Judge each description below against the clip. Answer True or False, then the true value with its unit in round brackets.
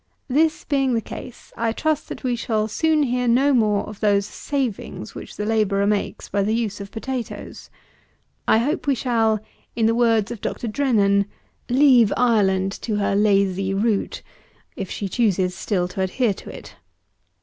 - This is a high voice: True (220 Hz)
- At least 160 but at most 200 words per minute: True (170 wpm)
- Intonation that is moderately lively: True (3.7 semitones)